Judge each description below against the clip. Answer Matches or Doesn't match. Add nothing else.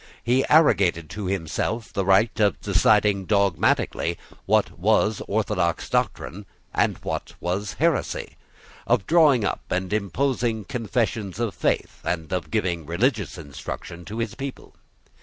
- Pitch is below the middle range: Matches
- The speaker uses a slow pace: Matches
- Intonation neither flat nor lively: Matches